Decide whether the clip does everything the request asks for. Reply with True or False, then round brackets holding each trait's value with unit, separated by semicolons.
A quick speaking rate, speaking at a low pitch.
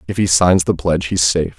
True (265 wpm; 85 Hz)